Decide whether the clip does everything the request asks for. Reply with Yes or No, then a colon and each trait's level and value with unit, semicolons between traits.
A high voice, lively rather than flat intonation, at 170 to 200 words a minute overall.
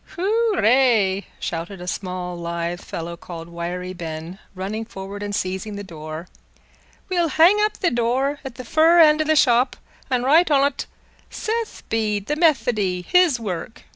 No: high, 215 Hz; wide, 8.9 semitones; average, 150 wpm